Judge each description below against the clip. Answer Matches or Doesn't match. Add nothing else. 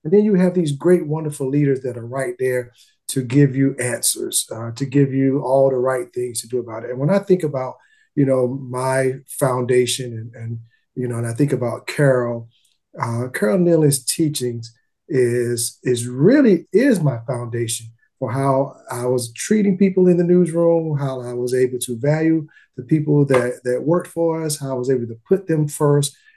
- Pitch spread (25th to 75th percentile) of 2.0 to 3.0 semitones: Doesn't match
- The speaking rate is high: Doesn't match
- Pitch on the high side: Doesn't match